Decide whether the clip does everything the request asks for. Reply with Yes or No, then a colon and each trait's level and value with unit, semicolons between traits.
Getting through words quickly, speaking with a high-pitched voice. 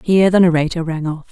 No: fast, 230 wpm; medium, 170 Hz